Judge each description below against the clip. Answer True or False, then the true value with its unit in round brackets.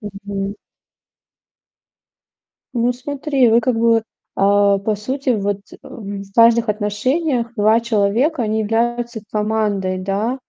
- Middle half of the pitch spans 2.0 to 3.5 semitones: True (2.9 semitones)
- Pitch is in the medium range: False (220 Hz)